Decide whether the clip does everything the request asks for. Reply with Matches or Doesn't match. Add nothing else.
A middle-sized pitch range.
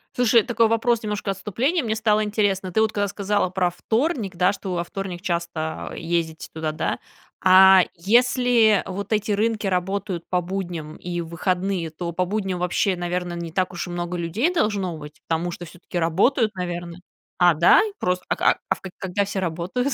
Matches